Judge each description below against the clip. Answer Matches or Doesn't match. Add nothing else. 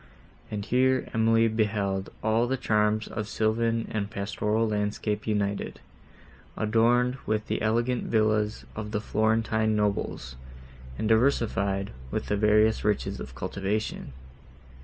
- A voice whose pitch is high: Doesn't match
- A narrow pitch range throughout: Matches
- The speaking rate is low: Matches